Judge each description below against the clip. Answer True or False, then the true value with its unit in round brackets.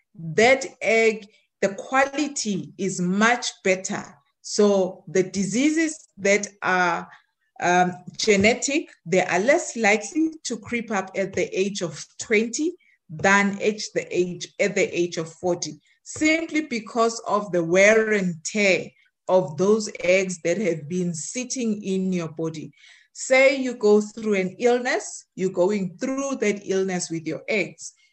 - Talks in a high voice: True (200 Hz)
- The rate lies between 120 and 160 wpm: True (140 wpm)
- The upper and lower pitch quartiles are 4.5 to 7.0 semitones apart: True (4.8 semitones)